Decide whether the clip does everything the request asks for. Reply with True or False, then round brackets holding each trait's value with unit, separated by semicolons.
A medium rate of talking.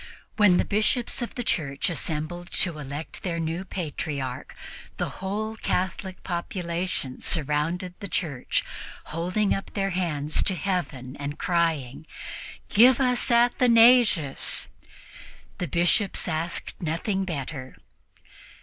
False (115 wpm)